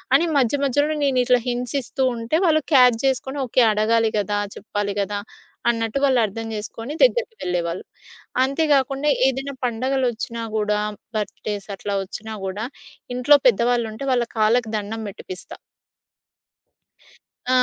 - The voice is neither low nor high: No, high, 235 Hz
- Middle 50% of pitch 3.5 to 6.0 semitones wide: Yes, average, 4.0 semitones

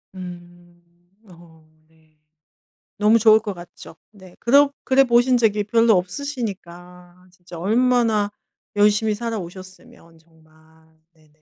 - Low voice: No, medium, 185 Hz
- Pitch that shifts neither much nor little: Yes, average, 4.5 semitones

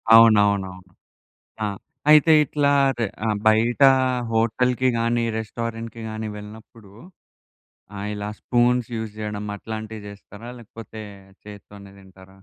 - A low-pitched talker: Yes, low, 110 Hz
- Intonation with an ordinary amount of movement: No, narrow, 2.2 semitones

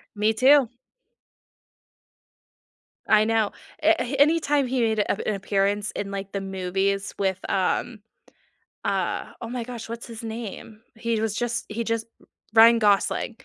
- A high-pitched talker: Yes, high, 220 Hz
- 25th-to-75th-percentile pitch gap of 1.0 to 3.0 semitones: Yes, average, 2.7 semitones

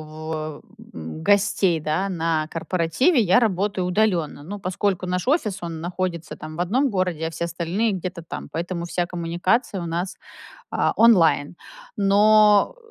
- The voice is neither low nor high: Yes, medium, 180 Hz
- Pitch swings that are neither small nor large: Yes, average, 3.5 semitones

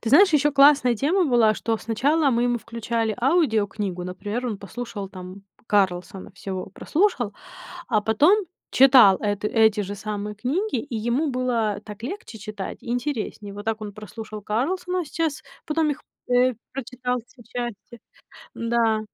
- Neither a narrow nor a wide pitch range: Yes, average, 4.4 semitones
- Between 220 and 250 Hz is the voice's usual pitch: Yes, high, 230 Hz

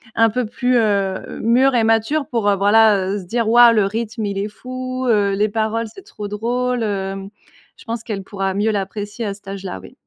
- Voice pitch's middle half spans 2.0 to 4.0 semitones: Yes, average, 2.8 semitones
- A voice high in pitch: Yes, high, 220 Hz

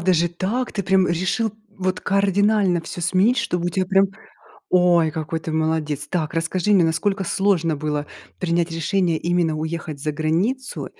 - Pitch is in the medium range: Yes, medium, 175 Hz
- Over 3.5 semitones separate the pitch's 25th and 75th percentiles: No, average, 3.1 semitones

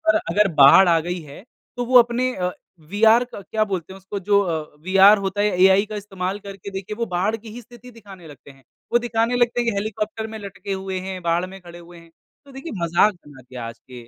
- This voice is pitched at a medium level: No, high, 195 Hz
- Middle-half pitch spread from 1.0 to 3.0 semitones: No, average, 4.0 semitones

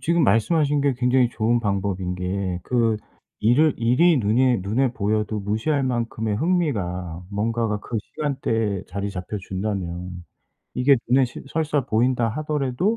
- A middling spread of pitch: Yes, average, 5.0 semitones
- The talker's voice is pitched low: Yes, low, 115 Hz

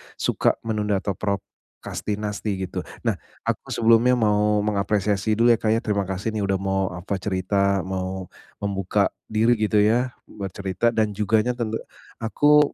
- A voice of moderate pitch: No, low, 105 Hz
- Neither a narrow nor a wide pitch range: No, narrow, 2.2 semitones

